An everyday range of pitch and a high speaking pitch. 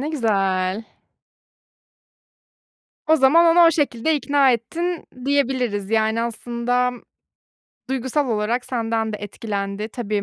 Yes: average, 4.7 semitones; high, 235 Hz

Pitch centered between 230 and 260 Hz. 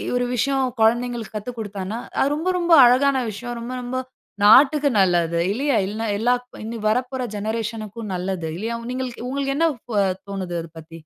Yes: high, 235 Hz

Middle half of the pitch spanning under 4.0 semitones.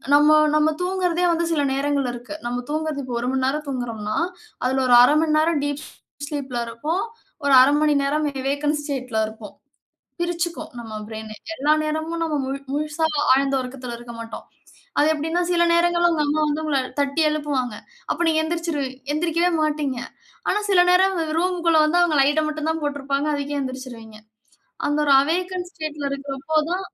Yes: average, 3.4 semitones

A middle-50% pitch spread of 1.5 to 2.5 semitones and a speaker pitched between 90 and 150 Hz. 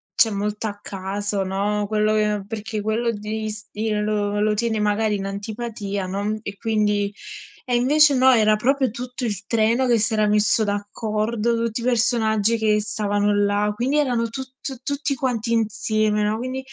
No: narrow, 2.1 semitones; high, 215 Hz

